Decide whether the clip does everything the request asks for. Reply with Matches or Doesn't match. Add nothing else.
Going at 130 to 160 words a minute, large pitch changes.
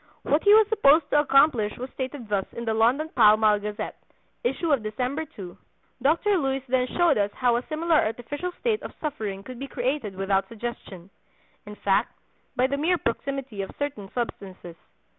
Doesn't match